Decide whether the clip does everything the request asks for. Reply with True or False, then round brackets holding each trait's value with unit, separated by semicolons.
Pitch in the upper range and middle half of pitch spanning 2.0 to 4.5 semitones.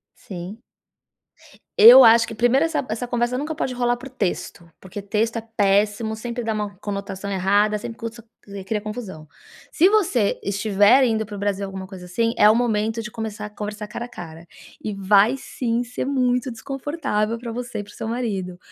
True (220 Hz; 3.1 semitones)